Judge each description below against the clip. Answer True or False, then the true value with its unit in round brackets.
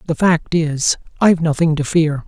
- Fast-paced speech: False (185 wpm)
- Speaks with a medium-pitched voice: True (160 Hz)